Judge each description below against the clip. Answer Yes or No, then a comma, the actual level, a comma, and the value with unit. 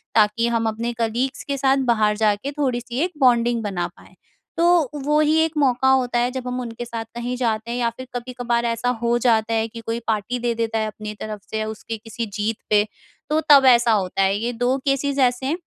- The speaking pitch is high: Yes, high, 235 Hz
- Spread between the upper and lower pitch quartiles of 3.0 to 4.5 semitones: No, narrow, 2.6 semitones